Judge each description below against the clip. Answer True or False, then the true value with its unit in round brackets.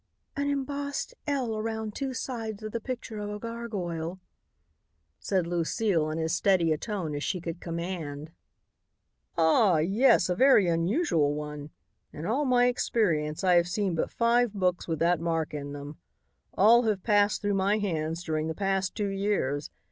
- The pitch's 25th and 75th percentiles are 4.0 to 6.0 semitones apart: True (5.3 semitones)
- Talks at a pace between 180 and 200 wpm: False (165 wpm)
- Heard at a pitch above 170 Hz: True (190 Hz)